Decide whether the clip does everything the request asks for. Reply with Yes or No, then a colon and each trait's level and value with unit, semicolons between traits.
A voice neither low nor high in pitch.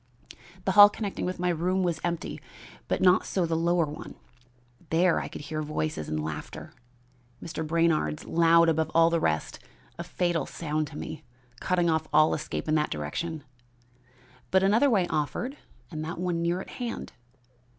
Yes: medium, 165 Hz